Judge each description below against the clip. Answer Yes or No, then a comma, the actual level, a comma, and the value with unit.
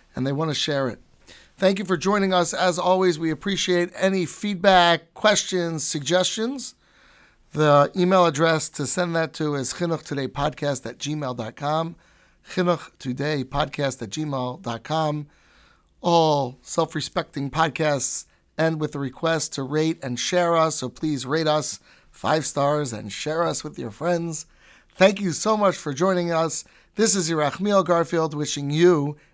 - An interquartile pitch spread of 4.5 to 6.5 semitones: No, average, 3.6 semitones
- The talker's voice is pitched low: No, medium, 160 Hz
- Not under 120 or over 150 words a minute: Yes, average, 145 wpm